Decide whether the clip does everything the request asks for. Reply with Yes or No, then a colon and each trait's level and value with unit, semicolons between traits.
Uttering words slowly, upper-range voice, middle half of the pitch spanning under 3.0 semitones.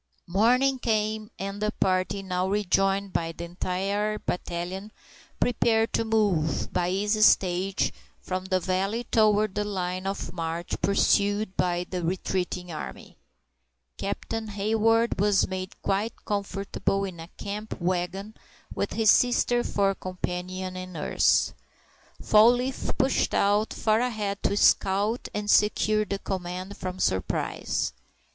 Yes: slow, 130 wpm; high, 195 Hz; narrow, 2.5 semitones